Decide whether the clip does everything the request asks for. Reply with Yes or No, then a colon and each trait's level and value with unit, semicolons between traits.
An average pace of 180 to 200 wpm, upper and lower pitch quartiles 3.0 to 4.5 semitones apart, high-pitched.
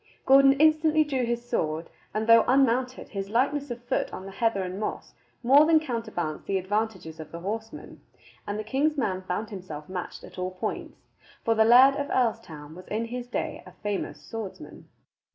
No: average, 185 wpm; wide, 5.5 semitones; high, 225 Hz